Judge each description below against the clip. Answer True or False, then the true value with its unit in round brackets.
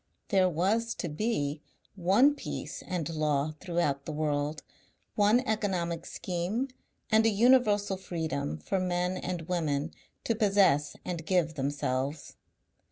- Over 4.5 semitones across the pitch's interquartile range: True (5.1 semitones)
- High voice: False (175 Hz)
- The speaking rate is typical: False (125 wpm)